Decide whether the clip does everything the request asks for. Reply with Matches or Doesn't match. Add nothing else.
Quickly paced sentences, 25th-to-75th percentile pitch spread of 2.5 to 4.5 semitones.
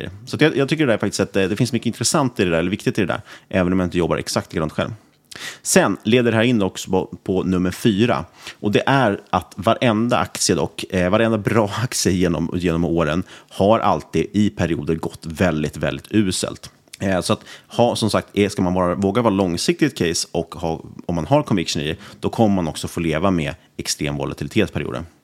Doesn't match